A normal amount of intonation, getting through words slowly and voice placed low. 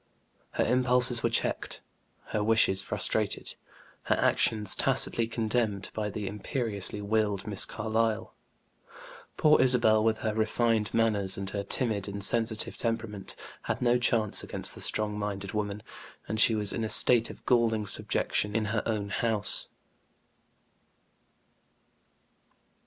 No: narrow, 1.8 semitones; slow, 130 wpm; low, 110 Hz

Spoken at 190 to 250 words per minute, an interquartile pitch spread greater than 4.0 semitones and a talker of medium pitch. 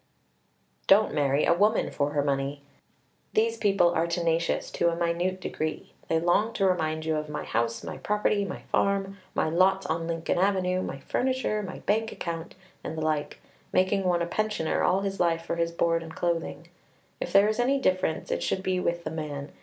No: average, 195 wpm; average, 3.4 semitones; medium, 175 Hz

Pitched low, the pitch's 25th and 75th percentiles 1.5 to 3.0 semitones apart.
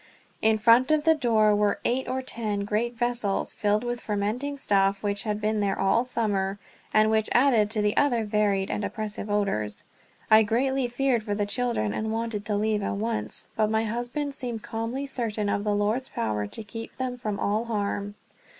No: high, 220 Hz; average, 2.7 semitones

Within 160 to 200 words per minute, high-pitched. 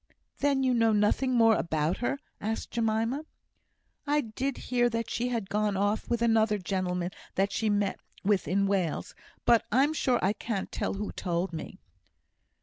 Yes: average, 165 wpm; high, 220 Hz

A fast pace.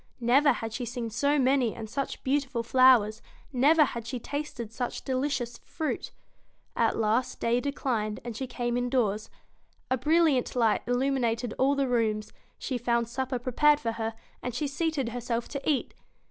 No: average, 165 wpm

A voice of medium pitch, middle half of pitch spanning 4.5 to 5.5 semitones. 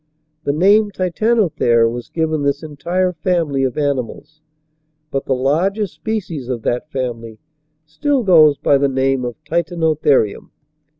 Yes: medium, 150 Hz; average, 5.1 semitones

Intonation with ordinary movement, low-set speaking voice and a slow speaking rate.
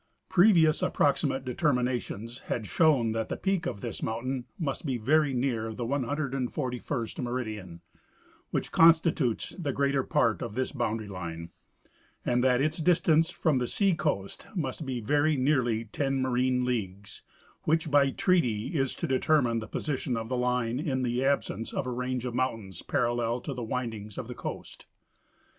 No: average, 3.8 semitones; low, 125 Hz; average, 155 wpm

